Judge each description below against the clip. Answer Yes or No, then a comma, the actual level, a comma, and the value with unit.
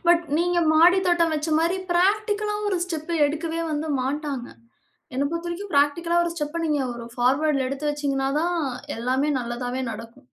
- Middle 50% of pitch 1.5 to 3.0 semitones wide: No, average, 4.1 semitones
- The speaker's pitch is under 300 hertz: No, very high, 310 Hz